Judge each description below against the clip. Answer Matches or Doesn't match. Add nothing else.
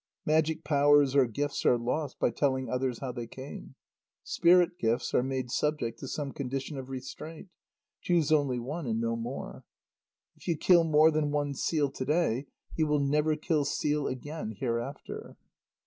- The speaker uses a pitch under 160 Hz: Matches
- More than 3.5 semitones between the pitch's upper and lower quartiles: Doesn't match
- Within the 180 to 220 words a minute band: Doesn't match